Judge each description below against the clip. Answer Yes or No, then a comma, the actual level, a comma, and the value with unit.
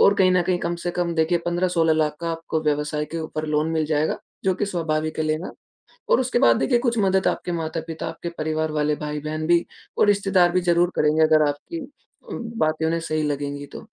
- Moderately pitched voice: Yes, medium, 160 Hz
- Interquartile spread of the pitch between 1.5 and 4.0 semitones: Yes, narrow, 2.4 semitones